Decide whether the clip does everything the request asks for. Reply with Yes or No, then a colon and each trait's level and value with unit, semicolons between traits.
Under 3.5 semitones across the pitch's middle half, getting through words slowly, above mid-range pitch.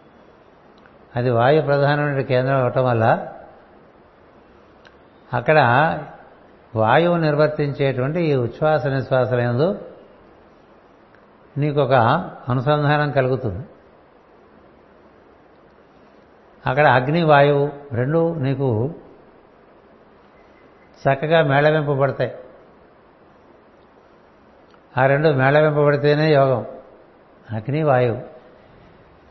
No: average, 2.9 semitones; slow, 60 wpm; medium, 140 Hz